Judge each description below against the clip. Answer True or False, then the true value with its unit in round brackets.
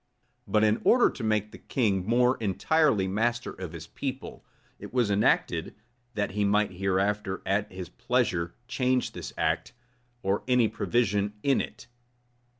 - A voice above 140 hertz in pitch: False (105 Hz)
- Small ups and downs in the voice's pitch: False (3.8 semitones)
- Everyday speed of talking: True (150 wpm)